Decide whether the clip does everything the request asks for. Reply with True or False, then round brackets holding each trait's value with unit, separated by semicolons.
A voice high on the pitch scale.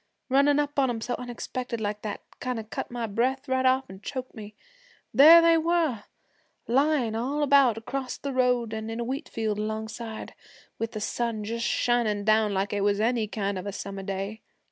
True (230 Hz)